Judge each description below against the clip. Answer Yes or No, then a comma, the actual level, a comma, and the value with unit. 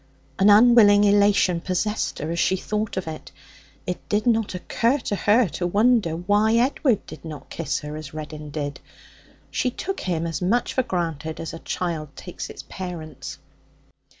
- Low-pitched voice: No, medium, 185 Hz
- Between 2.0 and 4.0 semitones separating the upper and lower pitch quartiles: No, average, 5.0 semitones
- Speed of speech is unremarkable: Yes, average, 170 wpm